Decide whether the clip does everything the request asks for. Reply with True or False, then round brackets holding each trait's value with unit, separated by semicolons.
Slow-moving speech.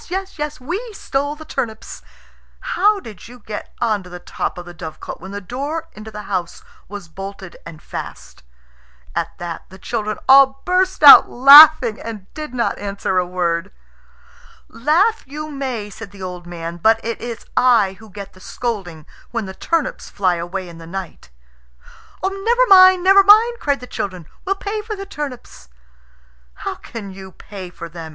False (175 wpm)